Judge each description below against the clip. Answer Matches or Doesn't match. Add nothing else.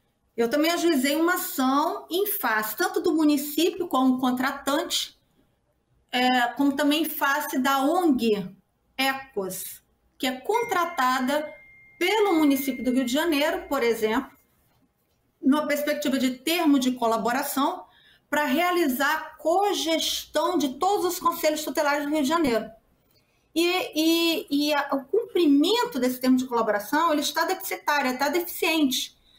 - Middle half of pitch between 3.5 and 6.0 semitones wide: Matches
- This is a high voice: Matches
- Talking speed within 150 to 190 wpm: Doesn't match